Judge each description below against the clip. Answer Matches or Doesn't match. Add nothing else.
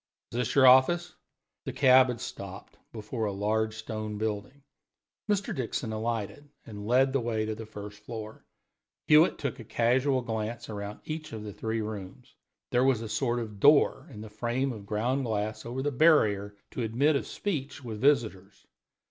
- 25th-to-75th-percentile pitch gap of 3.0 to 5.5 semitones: Matches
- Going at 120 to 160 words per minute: Doesn't match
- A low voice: Matches